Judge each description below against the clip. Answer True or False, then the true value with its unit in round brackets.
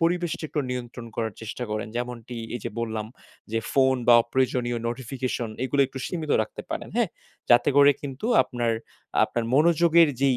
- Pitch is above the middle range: False (125 Hz)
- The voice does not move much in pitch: False (3.3 semitones)